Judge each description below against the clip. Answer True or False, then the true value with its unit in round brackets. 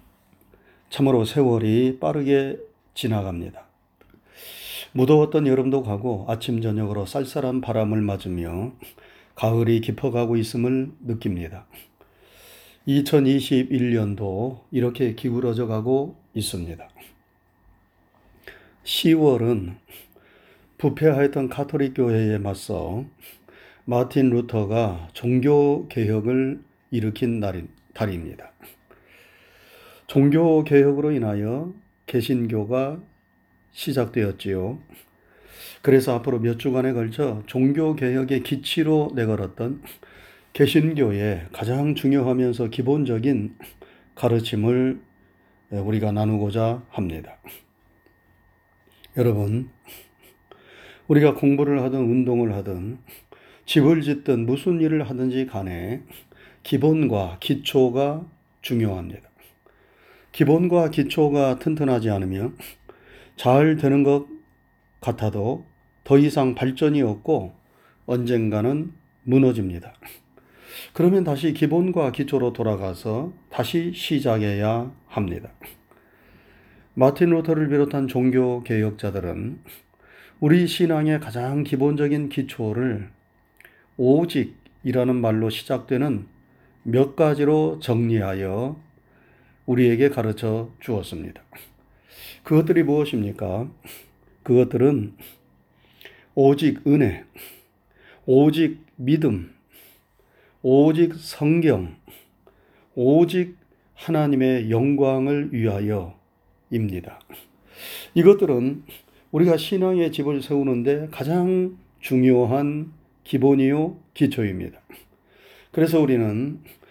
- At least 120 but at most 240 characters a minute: True (210 characters per minute)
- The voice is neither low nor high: False (130 Hz)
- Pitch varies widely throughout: False (4.8 semitones)